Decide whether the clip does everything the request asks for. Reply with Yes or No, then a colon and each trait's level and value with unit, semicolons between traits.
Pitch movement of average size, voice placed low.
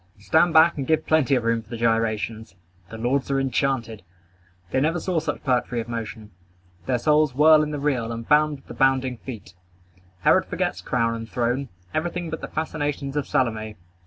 Yes: average, 4.6 semitones; low, 130 Hz